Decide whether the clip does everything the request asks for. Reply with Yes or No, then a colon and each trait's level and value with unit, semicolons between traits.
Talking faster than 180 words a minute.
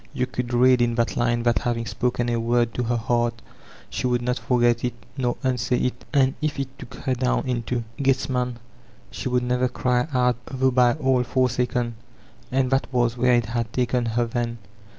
Yes: average, 190 wpm